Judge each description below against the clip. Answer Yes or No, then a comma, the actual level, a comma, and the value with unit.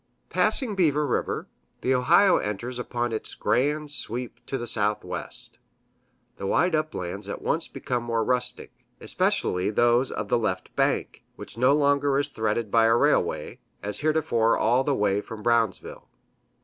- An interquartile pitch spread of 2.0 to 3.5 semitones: No, average, 4.3 semitones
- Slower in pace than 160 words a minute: Yes, average, 150 wpm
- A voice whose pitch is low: Yes, low, 120 Hz